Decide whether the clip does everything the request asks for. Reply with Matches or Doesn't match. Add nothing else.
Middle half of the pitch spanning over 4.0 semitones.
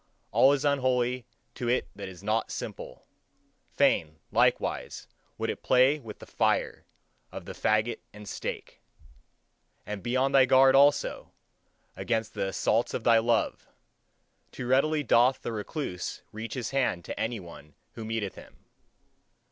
Doesn't match